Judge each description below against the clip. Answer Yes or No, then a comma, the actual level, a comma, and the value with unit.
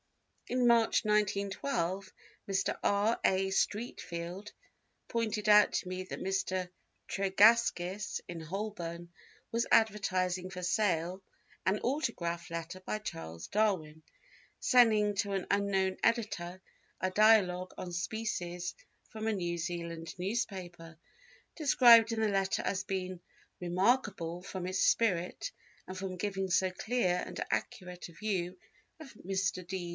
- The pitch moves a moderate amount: Yes, average, 3.0 semitones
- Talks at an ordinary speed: No, slow, 125 wpm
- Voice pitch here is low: No, high, 190 Hz